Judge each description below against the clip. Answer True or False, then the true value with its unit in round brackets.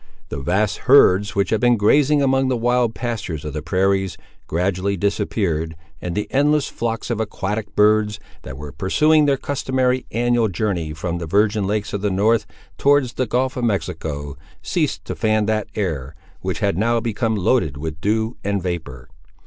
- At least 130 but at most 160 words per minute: False (175 wpm)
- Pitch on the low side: True (105 Hz)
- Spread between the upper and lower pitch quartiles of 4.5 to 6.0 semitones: True (4.8 semitones)